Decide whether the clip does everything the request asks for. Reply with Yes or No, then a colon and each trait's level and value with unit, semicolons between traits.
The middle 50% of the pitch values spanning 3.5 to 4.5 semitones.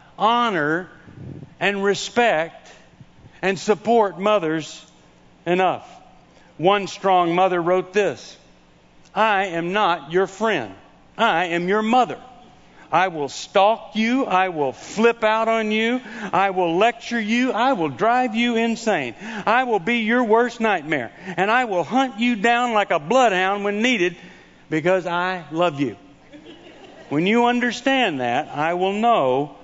No: average, 5.1 semitones